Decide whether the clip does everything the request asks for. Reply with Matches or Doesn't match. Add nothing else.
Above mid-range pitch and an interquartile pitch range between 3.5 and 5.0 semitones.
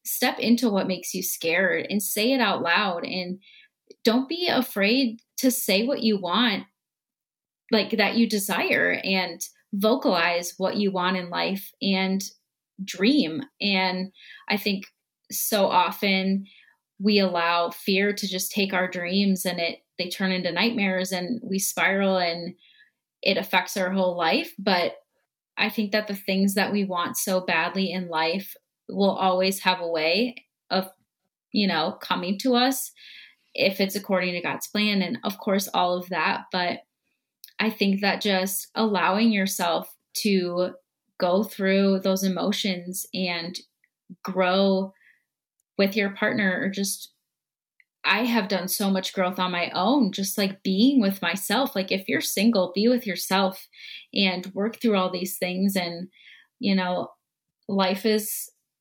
Doesn't match